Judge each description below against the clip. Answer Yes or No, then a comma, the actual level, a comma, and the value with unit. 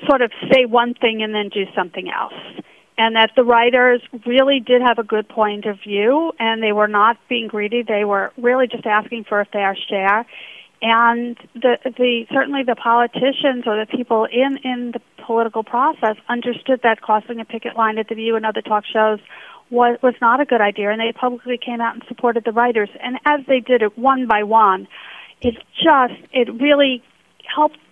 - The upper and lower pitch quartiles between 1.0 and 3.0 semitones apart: Yes, narrow, 2.5 semitones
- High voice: Yes, high, 235 Hz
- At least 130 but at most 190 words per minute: No, average, 200 wpm